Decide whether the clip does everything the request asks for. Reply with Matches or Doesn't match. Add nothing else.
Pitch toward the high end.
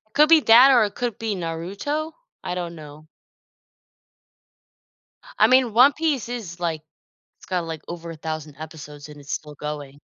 Doesn't match